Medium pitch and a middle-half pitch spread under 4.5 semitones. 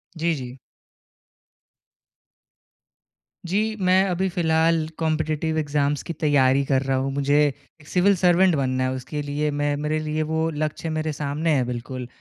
Yes: medium, 150 Hz; narrow, 2.4 semitones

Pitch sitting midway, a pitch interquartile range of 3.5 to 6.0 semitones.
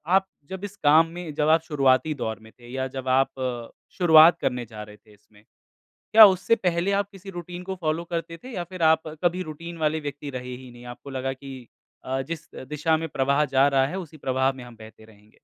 Yes: medium, 150 Hz; average, 4.6 semitones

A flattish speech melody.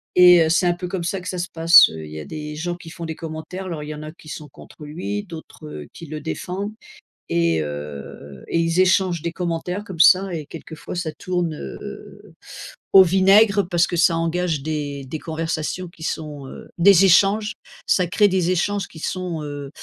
No: average, 3.0 semitones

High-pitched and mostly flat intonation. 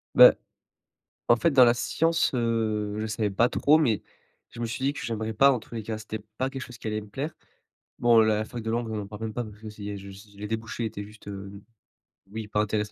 No: low, 110 Hz; narrow, 2.1 semitones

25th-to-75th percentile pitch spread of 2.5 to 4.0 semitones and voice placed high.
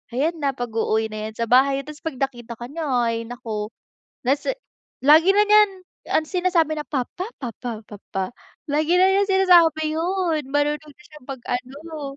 No: average, 5.3 semitones; very high, 290 Hz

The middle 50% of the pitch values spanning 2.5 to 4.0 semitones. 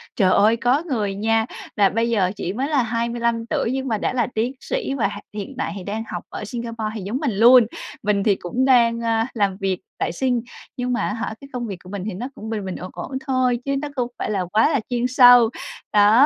Yes: average, 3.2 semitones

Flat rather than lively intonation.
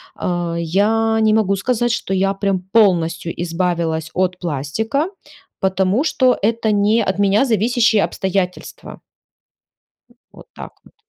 No: average, 3.8 semitones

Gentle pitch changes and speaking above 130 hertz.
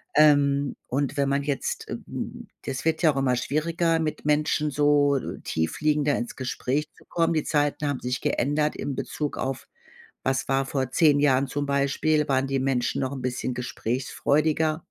Yes: narrow, 2.2 semitones; medium, 140 Hz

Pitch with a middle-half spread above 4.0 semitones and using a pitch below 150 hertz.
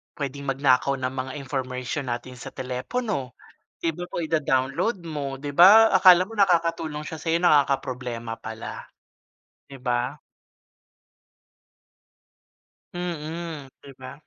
Yes: average, 4.4 semitones; medium, 140 Hz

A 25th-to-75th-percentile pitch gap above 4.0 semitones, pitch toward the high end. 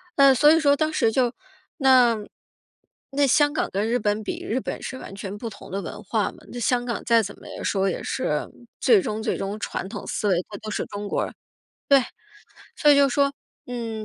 Yes: average, 4.9 semitones; high, 235 Hz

